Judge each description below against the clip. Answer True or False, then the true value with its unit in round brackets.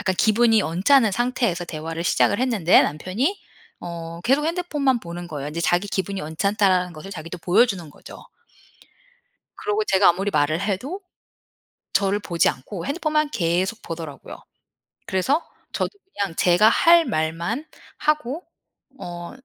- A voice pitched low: False (195 Hz)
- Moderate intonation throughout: False (6.5 semitones)